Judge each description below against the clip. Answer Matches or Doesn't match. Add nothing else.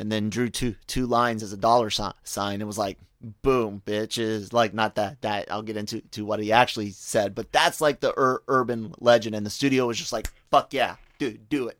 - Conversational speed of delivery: Doesn't match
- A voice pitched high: Doesn't match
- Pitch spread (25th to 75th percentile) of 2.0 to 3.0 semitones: Matches